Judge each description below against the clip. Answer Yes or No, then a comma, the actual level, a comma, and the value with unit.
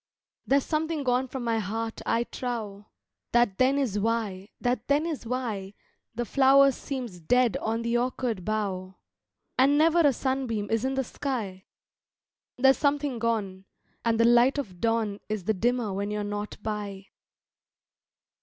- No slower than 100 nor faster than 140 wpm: No, average, 155 wpm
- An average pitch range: Yes, average, 4.1 semitones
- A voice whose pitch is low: No, high, 230 Hz